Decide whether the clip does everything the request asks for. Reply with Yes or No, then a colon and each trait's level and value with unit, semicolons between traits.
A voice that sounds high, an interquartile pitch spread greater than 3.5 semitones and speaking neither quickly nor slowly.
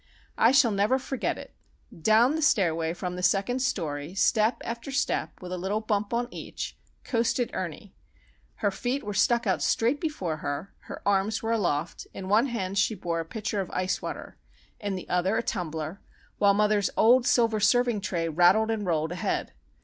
Yes: high, 205 Hz; average, 4.5 semitones; average, 180 wpm